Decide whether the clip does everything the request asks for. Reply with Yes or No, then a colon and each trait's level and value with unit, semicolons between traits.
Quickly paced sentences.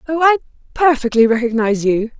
No: slow, 135 wpm